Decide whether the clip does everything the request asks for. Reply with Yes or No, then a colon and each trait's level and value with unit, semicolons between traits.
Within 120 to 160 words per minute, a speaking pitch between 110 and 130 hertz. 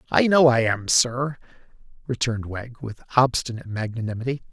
Yes: slow, 135 wpm; low, 120 Hz